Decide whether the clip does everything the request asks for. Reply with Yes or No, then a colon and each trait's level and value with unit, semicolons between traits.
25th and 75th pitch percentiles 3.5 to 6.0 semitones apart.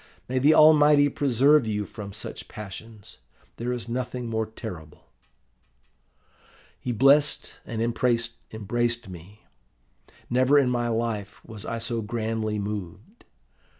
No: average, 3.0 semitones